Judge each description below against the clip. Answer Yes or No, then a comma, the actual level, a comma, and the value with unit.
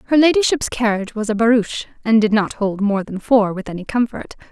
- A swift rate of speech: Yes, fast, 215 wpm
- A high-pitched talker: Yes, high, 220 Hz